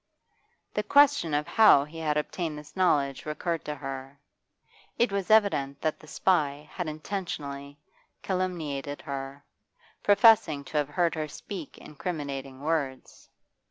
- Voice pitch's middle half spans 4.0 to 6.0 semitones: Yes, average, 4.4 semitones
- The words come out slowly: Yes, slow, 130 wpm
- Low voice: No, medium, 150 Hz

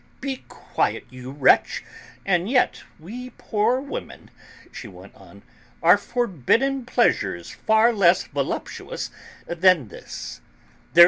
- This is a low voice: No, high, 195 Hz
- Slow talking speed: Yes, slow, 110 wpm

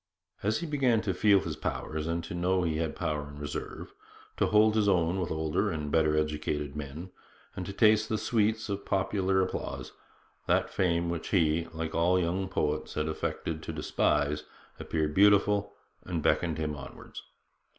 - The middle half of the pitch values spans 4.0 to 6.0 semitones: Yes, average, 4.4 semitones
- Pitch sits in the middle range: No, very low, 85 Hz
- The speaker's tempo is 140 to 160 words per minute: No, average, 175 wpm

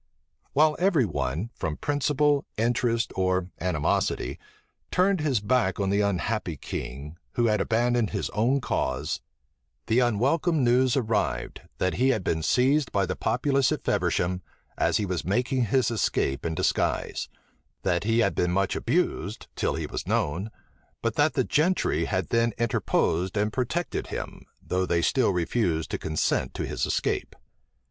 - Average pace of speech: Yes, average, 155 wpm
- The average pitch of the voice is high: No, low, 110 Hz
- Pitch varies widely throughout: Yes, wide, 5.7 semitones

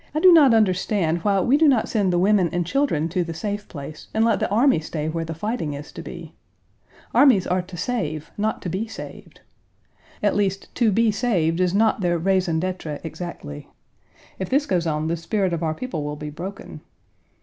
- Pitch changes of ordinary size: Yes, average, 4.9 semitones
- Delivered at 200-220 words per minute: Yes, fast, 205 wpm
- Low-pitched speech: No, medium, 185 Hz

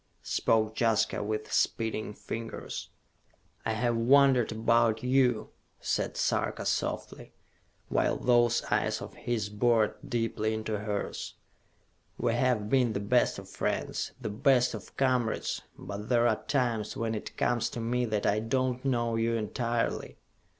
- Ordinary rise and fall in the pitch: No, narrow, 2.1 semitones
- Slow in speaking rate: No, average, 145 wpm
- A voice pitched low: Yes, low, 115 Hz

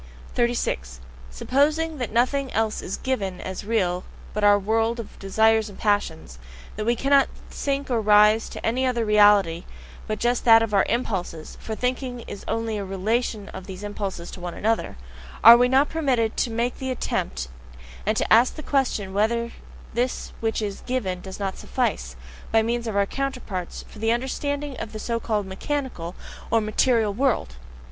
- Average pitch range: Yes, average, 3.7 semitones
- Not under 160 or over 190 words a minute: Yes, average, 175 wpm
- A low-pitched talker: No, high, 225 Hz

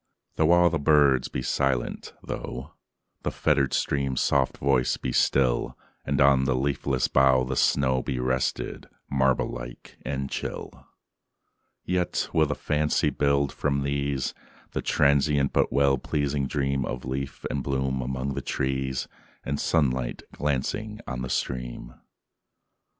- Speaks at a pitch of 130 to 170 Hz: No, very low, 70 Hz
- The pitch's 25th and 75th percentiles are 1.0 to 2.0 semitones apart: Yes, narrow, 1.5 semitones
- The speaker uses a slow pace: Yes, slow, 115 wpm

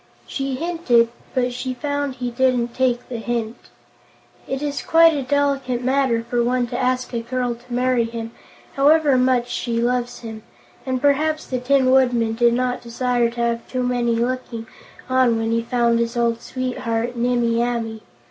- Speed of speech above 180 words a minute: No, average, 170 wpm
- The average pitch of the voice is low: No, high, 245 Hz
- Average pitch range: No, narrow, 1.7 semitones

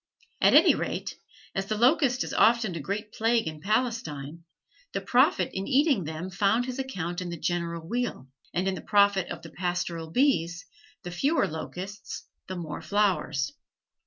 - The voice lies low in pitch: No, high, 190 Hz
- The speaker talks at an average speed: Yes, average, 165 wpm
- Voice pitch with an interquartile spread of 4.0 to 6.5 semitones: Yes, average, 5.3 semitones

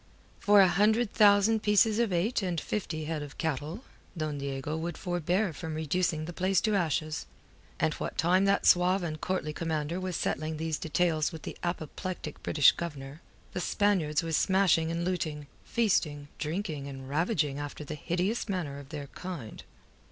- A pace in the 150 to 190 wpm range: Yes, average, 165 wpm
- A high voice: No, medium, 165 Hz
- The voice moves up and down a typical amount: Yes, average, 3.6 semitones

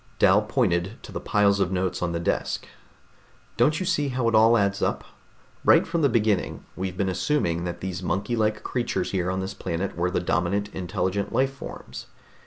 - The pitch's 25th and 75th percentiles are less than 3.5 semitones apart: No, average, 4.1 semitones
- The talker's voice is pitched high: No, low, 100 Hz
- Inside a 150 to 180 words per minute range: No, average, 190 wpm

